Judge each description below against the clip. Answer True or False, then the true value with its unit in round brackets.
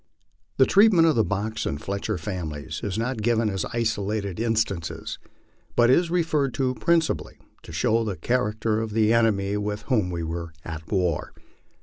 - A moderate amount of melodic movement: True (4.2 semitones)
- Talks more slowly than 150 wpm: False (165 wpm)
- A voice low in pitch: True (110 Hz)